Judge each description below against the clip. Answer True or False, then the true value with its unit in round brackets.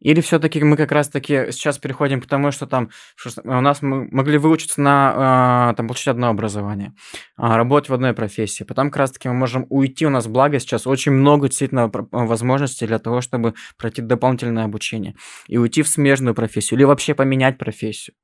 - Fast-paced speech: True (180 wpm)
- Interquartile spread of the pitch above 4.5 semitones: False (3.2 semitones)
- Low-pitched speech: True (130 Hz)